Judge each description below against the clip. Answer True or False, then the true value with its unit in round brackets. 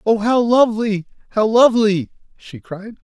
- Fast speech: False (135 wpm)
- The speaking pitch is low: False (215 Hz)